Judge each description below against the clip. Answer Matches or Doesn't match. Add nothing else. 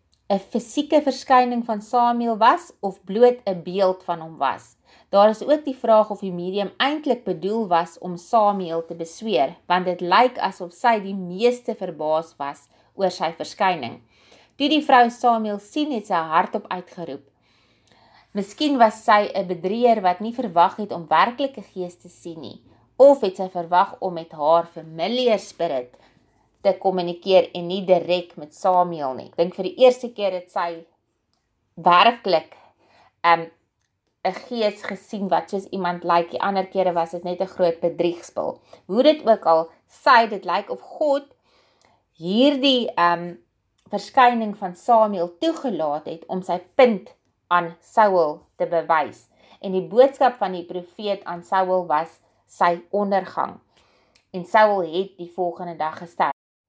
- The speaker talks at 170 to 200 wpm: Doesn't match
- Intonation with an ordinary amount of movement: Matches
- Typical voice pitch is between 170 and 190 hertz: Matches